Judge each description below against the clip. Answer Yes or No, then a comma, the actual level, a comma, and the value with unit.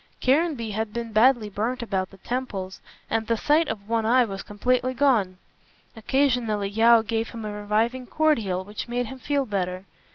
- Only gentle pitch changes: No, average, 3.5 semitones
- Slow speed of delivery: No, average, 170 wpm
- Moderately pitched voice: No, high, 225 Hz